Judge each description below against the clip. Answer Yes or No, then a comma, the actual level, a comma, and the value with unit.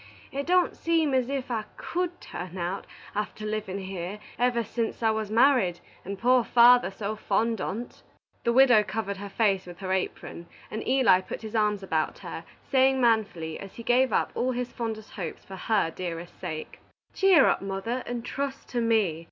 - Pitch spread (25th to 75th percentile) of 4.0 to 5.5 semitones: Yes, average, 4.4 semitones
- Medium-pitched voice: No, high, 220 Hz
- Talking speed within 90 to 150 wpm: No, average, 185 wpm